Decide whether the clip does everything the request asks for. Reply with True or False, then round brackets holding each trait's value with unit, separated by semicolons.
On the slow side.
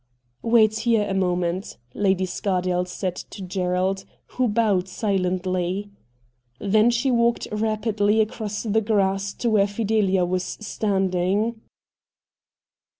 True (110 wpm)